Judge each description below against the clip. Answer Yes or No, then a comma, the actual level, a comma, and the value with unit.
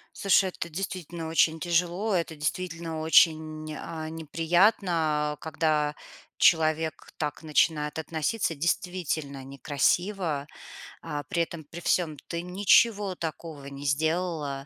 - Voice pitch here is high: No, medium, 160 Hz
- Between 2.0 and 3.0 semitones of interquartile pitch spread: Yes, narrow, 2.5 semitones